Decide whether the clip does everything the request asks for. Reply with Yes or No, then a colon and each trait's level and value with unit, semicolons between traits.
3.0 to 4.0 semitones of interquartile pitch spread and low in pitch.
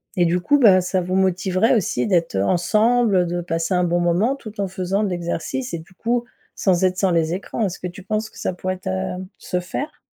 No: average, 3.3 semitones; medium, 185 Hz